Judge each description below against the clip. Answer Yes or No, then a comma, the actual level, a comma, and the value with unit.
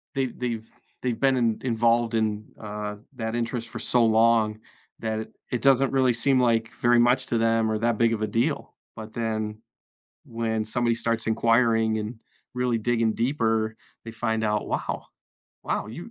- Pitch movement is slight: Yes, narrow, 1.4 semitones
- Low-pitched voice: Yes, low, 115 Hz